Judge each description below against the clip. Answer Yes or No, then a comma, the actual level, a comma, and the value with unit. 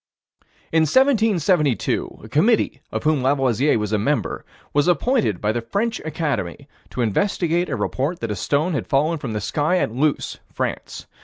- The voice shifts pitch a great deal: Yes, wide, 6.6 semitones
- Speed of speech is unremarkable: Yes, average, 165 wpm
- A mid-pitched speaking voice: Yes, medium, 150 Hz